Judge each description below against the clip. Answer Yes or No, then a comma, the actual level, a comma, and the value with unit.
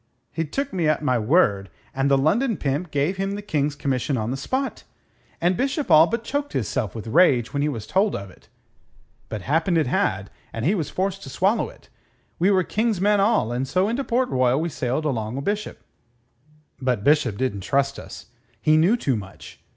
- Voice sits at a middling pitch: Yes, medium, 150 Hz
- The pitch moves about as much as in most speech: No, wide, 7.4 semitones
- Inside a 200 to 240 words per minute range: Yes, fast, 205 wpm